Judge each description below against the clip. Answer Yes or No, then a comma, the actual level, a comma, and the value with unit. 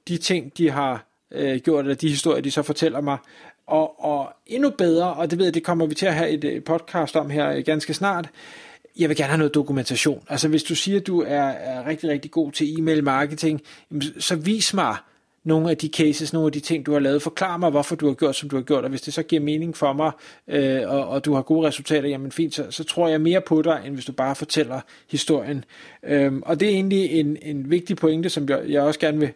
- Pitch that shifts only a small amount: Yes, narrow, 2.2 semitones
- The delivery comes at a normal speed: No, fast, 245 wpm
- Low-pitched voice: No, medium, 155 Hz